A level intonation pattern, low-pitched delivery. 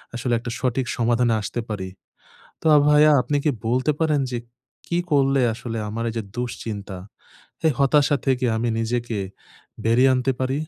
No: average, 3.0 semitones; low, 125 Hz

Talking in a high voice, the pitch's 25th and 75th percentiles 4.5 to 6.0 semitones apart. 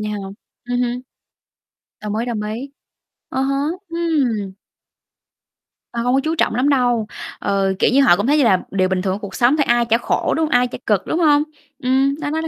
Yes: high, 245 Hz; average, 4.9 semitones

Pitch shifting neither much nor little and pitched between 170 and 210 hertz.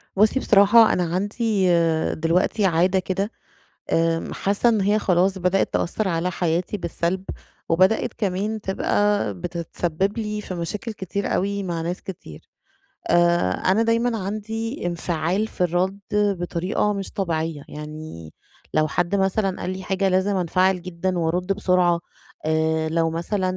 Yes: average, 3.0 semitones; medium, 185 Hz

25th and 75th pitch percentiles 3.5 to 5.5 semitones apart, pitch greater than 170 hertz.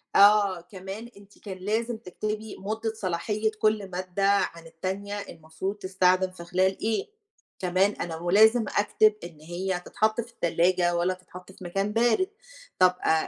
No: average, 3.0 semitones; high, 190 Hz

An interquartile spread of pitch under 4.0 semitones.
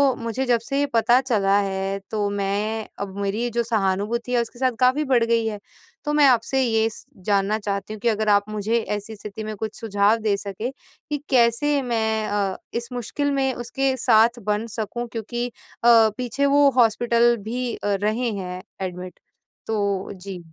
Yes: average, 2.9 semitones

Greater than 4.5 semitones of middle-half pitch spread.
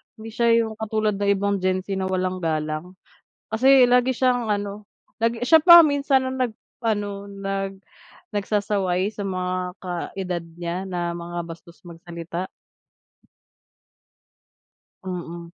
No: average, 3.6 semitones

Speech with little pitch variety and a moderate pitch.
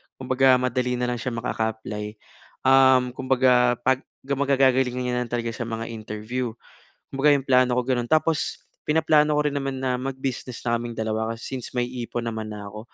No: narrow, 2.2 semitones; low, 125 Hz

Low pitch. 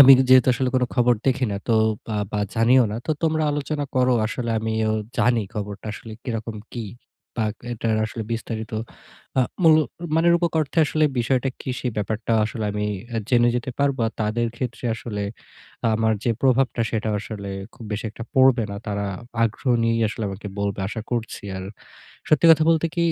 Yes: low, 115 Hz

